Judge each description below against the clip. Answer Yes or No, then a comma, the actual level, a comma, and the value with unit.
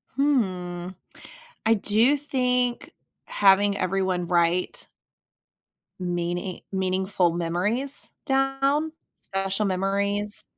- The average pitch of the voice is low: No, high, 195 Hz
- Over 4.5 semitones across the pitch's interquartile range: Yes, average, 5.3 semitones